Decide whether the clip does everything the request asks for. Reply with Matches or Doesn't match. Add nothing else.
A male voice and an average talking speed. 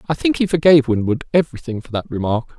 Doesn't match